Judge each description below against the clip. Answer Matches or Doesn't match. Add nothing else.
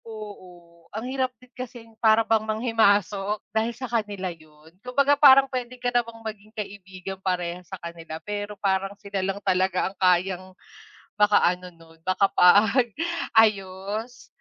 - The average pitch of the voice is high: Matches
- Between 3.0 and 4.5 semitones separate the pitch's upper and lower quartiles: Matches